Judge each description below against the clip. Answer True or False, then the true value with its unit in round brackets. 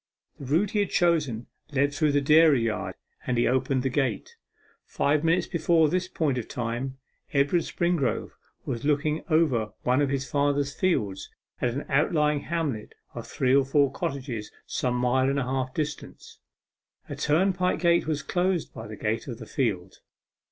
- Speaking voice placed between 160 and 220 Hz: False (140 Hz)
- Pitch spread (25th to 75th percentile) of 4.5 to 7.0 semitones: False (4.0 semitones)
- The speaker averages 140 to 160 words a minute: False (170 wpm)